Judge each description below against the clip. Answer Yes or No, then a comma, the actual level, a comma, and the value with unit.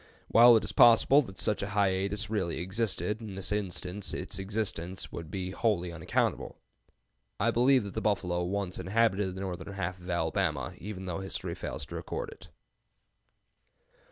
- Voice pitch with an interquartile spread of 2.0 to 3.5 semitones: Yes, average, 2.8 semitones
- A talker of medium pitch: No, very low, 95 Hz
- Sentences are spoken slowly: No, average, 160 wpm